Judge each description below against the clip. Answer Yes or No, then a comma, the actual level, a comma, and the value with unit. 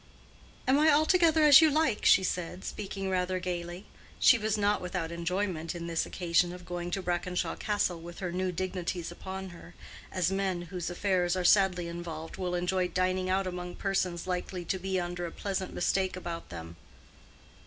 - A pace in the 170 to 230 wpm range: Yes, average, 175 wpm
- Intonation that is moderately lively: No, narrow, 1.8 semitones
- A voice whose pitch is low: No, medium, 180 Hz